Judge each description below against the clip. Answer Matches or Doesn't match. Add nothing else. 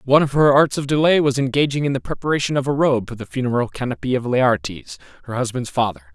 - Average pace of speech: Doesn't match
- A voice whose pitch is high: Doesn't match